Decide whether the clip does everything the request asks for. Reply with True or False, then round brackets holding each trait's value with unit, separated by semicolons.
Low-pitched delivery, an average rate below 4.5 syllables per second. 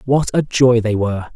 False (120 Hz; 5.3 syllables/s)